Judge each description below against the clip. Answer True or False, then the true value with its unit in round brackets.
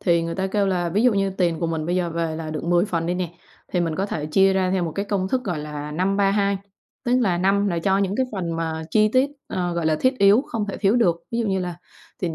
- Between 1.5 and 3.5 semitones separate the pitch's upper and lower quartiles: True (3.0 semitones)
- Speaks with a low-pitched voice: False (185 Hz)